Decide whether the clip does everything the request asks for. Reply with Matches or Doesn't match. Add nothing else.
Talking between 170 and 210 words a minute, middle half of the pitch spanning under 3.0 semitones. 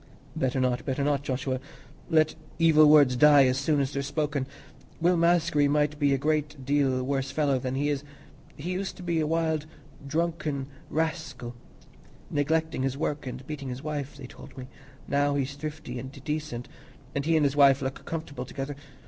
Matches